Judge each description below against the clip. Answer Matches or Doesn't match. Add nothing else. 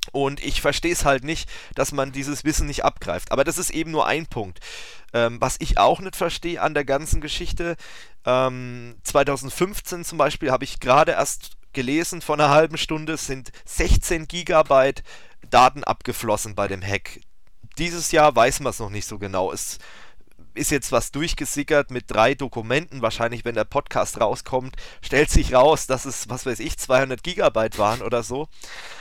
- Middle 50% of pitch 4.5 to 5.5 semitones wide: Matches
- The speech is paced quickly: Doesn't match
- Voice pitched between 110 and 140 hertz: Matches